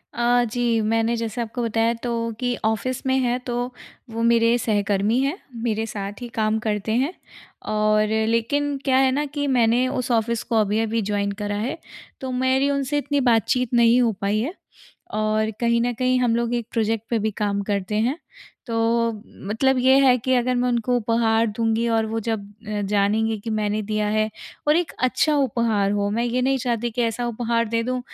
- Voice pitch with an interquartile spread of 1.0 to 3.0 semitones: Yes, narrow, 2.5 semitones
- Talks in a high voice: Yes, high, 230 Hz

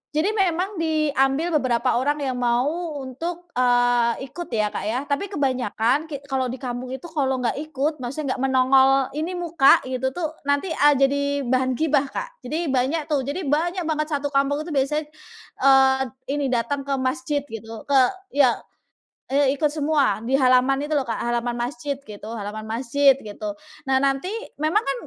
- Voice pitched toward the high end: Yes, very high, 275 Hz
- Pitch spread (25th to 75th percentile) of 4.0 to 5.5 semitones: No, average, 3.3 semitones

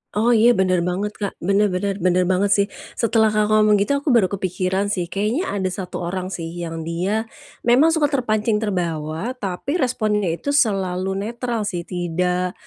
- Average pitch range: Yes, average, 3.3 semitones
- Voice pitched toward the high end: Yes, high, 200 Hz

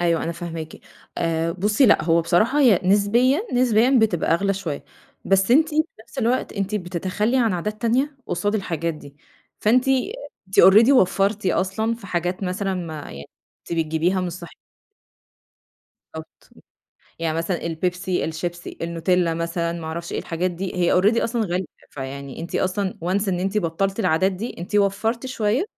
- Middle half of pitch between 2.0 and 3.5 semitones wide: No, average, 4.2 semitones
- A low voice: No, medium, 185 Hz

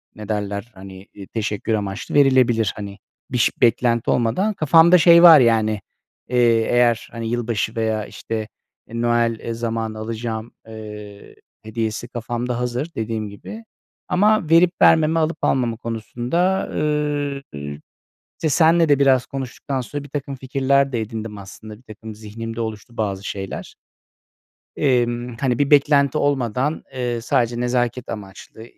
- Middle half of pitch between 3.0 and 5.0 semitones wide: Yes, average, 3.7 semitones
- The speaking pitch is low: Yes, low, 120 Hz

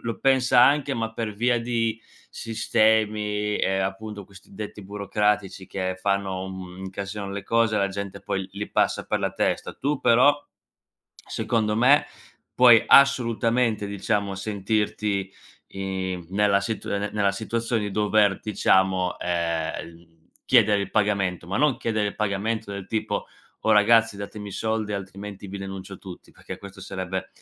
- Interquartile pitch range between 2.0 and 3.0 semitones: Yes, narrow, 2.4 semitones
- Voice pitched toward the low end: Yes, low, 105 Hz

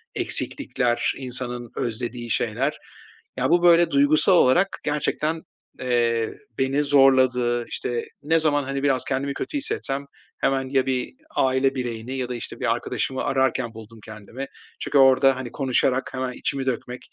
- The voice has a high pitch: No, low, 130 Hz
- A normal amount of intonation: No, narrow, 2.3 semitones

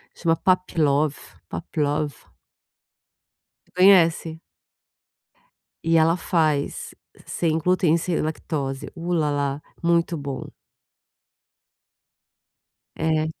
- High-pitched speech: No, medium, 160 Hz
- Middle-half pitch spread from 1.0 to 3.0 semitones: Yes, narrow, 2.4 semitones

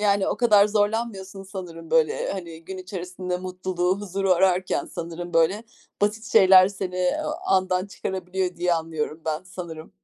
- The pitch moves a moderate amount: No, narrow, 2.0 semitones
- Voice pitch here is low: No, medium, 185 Hz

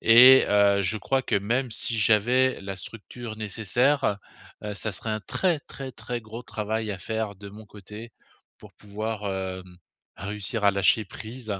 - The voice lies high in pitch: No, low, 110 Hz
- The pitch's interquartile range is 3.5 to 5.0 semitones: No, narrow, 2.6 semitones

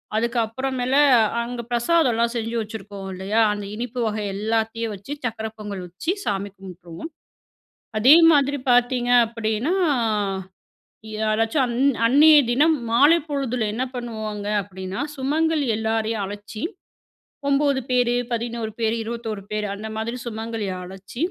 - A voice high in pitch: Yes, high, 225 Hz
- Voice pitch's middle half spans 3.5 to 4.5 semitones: No, average, 2.7 semitones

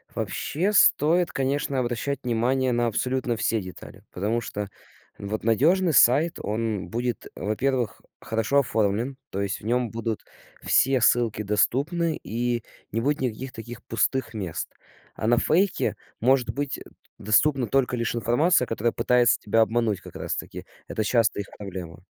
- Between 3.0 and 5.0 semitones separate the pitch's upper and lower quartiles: Yes, average, 3.4 semitones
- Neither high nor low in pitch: No, low, 120 Hz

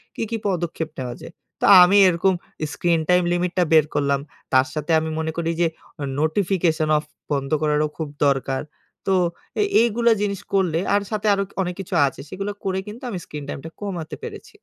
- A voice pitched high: No, medium, 170 Hz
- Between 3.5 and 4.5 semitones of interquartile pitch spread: Yes, average, 4.2 semitones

